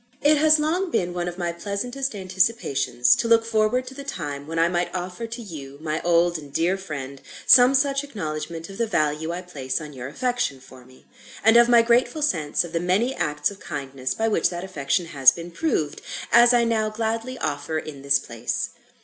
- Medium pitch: Yes, medium, 180 Hz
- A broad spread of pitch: Yes, wide, 7.7 semitones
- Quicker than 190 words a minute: Yes, fast, 205 wpm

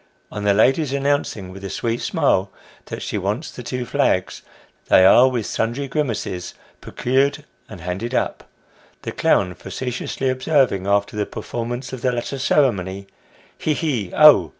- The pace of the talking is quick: No, average, 155 wpm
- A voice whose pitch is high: No, low, 120 Hz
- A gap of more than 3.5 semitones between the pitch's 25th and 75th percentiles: Yes, average, 5.1 semitones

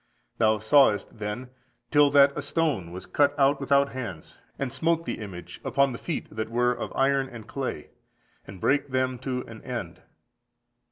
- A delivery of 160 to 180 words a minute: Yes, average, 170 wpm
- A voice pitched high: No, low, 130 Hz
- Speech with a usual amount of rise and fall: Yes, average, 4.1 semitones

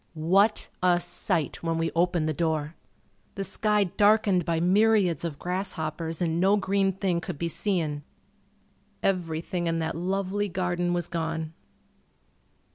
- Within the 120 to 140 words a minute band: Yes, slow, 135 wpm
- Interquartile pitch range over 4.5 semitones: No, average, 2.9 semitones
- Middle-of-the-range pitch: Yes, medium, 175 Hz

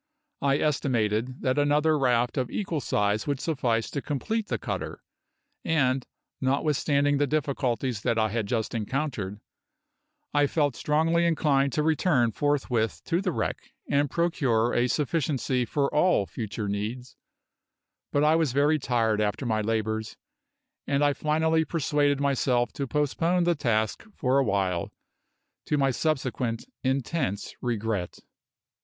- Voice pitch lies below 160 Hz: Yes, low, 135 Hz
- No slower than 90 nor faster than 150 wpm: Yes, slow, 135 wpm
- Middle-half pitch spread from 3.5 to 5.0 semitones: Yes, average, 4.6 semitones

